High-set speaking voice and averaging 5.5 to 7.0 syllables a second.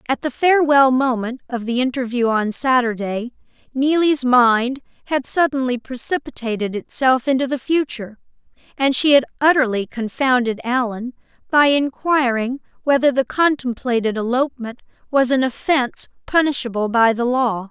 No: very high, 255 Hz; 4.9 syllables/s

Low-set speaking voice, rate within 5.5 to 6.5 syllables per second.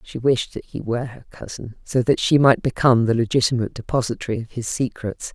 Yes: low, 120 Hz; 6.0 syllables/s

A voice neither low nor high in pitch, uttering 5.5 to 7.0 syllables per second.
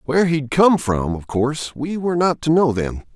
No: medium, 145 Hz; 5.1 syllables/s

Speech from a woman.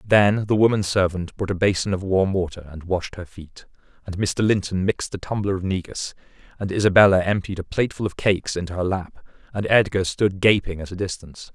No: male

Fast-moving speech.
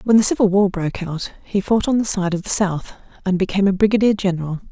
Yes: fast, 240 wpm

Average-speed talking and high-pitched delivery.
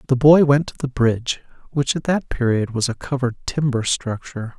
No: average, 195 wpm; low, 130 Hz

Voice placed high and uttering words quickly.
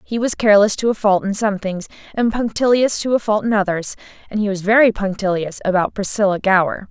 Yes: high, 205 Hz; fast, 210 wpm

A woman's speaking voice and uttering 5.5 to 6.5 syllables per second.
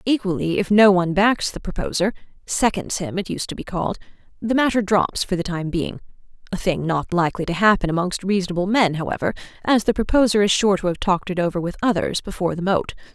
Yes: female; 6.2 syllables/s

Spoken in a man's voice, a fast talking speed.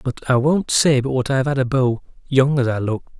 Yes: male; fast, 265 wpm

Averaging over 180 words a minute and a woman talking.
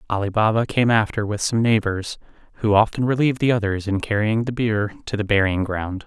No: average, 200 wpm; male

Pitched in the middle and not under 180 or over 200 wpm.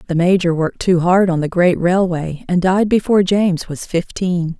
Yes: medium, 175 Hz; average, 195 wpm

